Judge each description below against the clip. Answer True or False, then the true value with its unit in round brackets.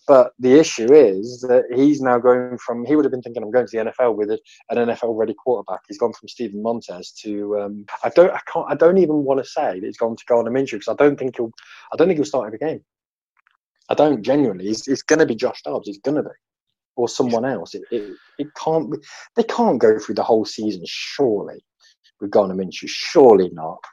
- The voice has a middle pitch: False (120 Hz)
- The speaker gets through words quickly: True (230 wpm)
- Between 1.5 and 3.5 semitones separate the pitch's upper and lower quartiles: False (4.4 semitones)